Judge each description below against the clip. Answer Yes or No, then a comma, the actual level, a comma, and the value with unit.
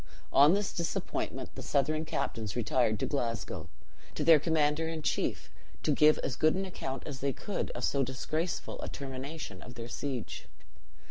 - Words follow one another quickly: No, average, 170 wpm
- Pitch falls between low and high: Yes, medium, 145 Hz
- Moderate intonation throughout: Yes, average, 4.1 semitones